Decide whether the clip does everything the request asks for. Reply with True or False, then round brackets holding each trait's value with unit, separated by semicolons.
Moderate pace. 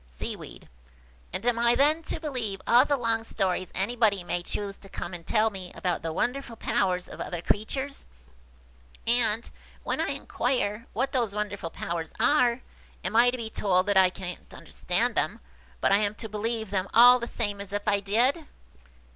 True (175 wpm)